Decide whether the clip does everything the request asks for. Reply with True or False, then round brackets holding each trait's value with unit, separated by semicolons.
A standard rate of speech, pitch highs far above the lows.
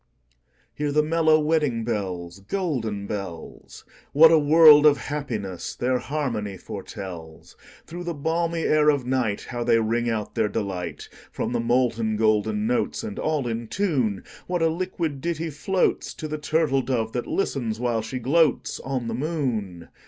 False (130 wpm; 6.1 semitones)